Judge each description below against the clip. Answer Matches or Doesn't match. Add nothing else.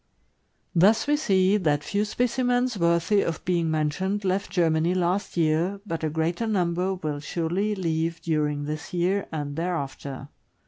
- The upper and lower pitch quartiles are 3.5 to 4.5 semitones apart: Matches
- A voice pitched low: Doesn't match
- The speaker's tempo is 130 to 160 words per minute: Matches